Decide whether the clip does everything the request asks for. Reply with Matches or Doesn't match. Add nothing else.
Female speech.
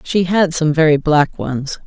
Matches